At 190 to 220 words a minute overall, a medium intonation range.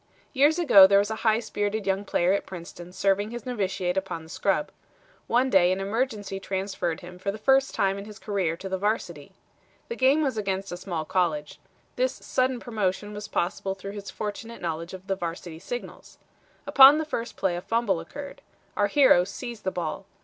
Yes: average, 195 wpm; average, 3.9 semitones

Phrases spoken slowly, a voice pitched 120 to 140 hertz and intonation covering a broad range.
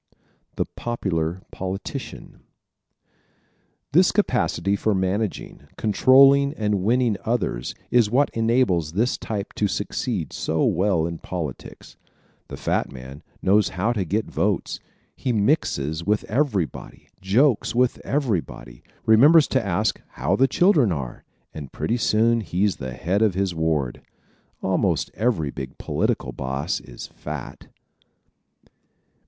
No: slow, 125 wpm; low, 100 Hz; wide, 6.3 semitones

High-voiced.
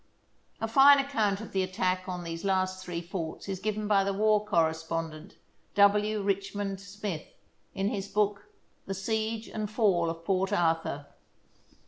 Yes: high, 195 Hz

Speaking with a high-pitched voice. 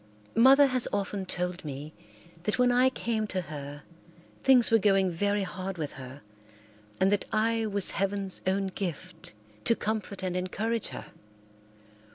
Yes: high, 195 Hz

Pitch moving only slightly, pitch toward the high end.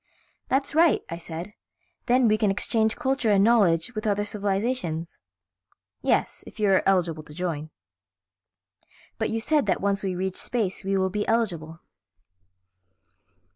No: average, 4.1 semitones; high, 200 Hz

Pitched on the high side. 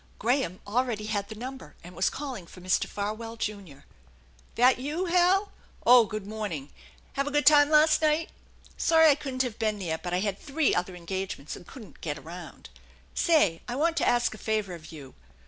Yes: high, 220 Hz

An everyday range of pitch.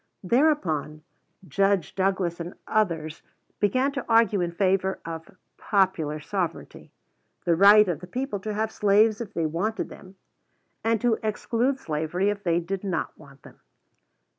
Yes: average, 4.3 semitones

